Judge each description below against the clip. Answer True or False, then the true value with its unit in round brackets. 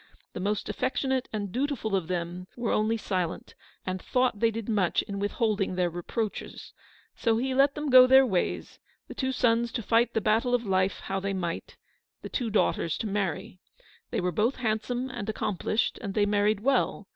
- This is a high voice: True (215 Hz)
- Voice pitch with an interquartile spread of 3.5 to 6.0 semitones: True (4.1 semitones)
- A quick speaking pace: False (190 wpm)